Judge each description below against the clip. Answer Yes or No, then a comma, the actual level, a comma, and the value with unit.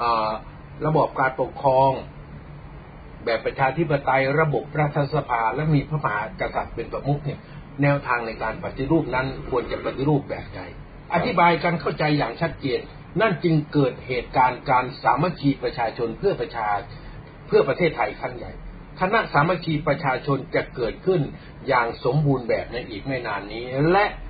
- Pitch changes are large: No, average, 3.6 semitones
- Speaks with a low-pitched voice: No, medium, 145 Hz